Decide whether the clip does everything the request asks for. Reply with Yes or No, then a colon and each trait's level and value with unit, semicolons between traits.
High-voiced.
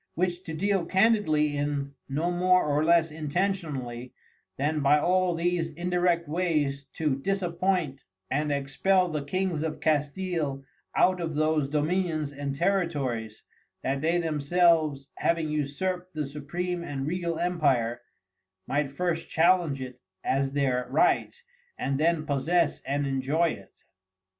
No: medium, 155 Hz